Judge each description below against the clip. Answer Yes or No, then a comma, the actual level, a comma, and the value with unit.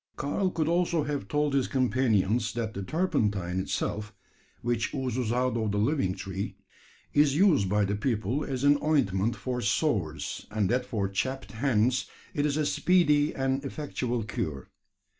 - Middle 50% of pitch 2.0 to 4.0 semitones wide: No, wide, 5.6 semitones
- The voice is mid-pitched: No, low, 125 Hz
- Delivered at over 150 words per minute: Yes, average, 160 wpm